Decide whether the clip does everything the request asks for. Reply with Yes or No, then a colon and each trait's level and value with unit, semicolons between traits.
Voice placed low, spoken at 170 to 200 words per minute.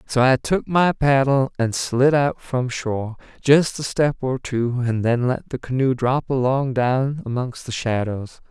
Yes: low, 130 Hz; average, 185 wpm